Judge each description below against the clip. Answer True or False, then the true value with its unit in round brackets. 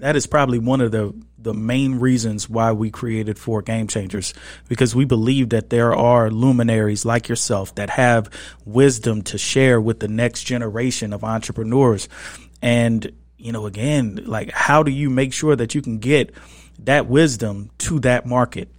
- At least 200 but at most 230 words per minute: False (170 wpm)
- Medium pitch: False (115 Hz)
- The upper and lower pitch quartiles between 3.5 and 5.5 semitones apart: False (2.9 semitones)